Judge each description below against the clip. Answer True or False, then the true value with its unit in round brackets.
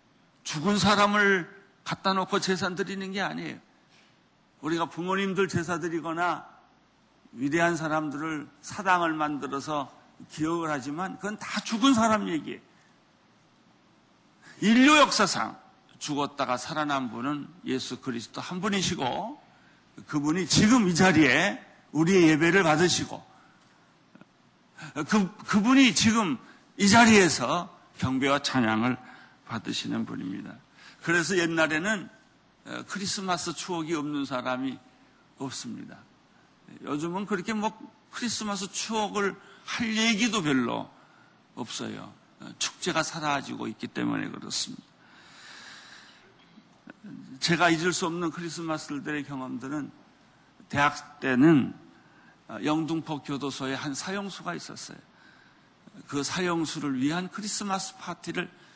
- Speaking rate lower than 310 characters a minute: True (255 characters per minute)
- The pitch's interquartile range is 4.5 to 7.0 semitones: True (5.2 semitones)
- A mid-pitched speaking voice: True (175 Hz)